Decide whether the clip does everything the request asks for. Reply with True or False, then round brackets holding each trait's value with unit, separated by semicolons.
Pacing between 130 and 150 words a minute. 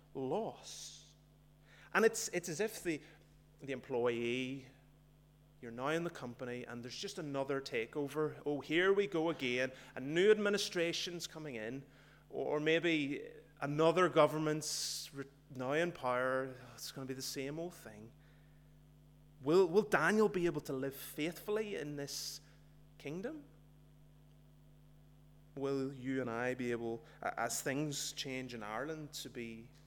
True (140 wpm)